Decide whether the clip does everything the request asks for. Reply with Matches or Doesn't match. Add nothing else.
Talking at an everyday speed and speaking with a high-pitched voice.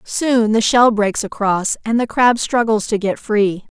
Matches